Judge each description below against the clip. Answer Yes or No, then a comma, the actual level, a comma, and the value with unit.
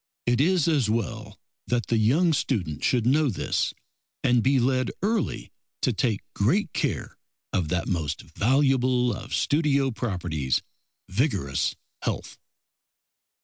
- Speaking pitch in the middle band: No, low, 120 Hz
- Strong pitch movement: Yes, wide, 5.8 semitones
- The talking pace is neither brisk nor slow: No, slow, 125 wpm